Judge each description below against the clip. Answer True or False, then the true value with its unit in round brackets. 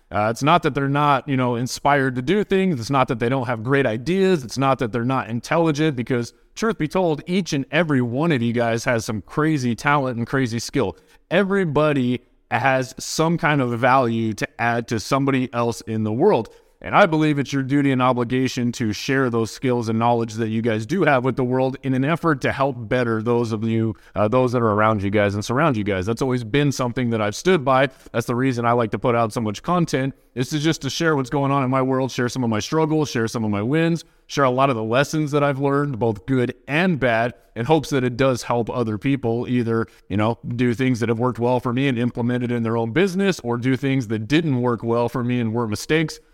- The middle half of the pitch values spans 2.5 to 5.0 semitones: True (3.4 semitones)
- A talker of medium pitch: False (130 Hz)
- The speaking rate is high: True (245 wpm)